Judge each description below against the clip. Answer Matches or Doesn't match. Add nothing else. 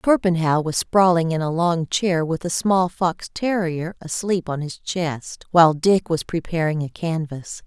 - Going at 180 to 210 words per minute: Doesn't match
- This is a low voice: Doesn't match